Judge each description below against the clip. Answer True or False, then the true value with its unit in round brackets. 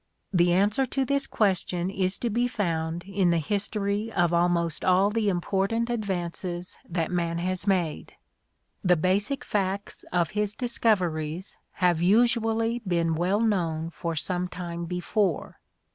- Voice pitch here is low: False (185 Hz)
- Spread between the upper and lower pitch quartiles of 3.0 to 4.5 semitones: True (3.5 semitones)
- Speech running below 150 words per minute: True (140 wpm)